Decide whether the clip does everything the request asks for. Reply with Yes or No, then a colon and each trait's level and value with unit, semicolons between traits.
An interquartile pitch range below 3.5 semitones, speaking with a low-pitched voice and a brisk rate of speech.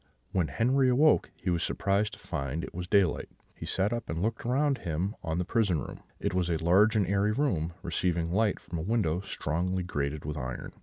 No: average, 4.7 semitones; very low, 90 Hz; fast, 210 wpm